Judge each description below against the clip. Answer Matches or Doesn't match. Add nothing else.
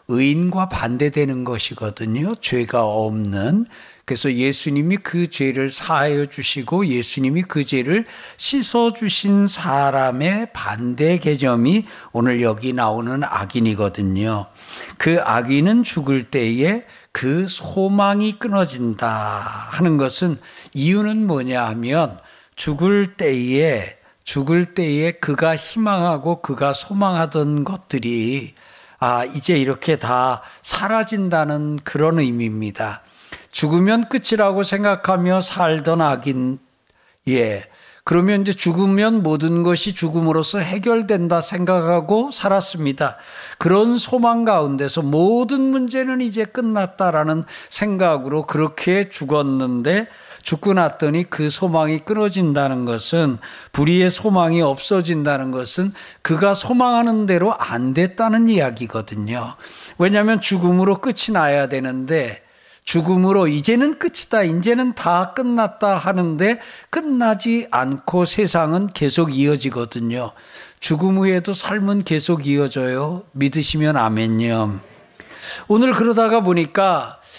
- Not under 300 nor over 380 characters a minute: Doesn't match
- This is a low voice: Doesn't match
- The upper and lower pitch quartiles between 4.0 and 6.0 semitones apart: Doesn't match